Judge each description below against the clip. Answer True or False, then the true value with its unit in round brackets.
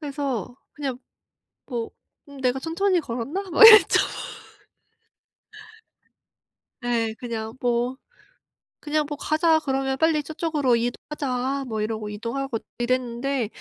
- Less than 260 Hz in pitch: False (265 Hz)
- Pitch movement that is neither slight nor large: True (4.1 semitones)